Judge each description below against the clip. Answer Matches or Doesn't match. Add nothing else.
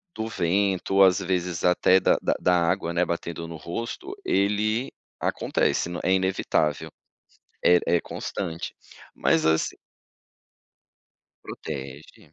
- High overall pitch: Doesn't match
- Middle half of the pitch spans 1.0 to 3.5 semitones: Matches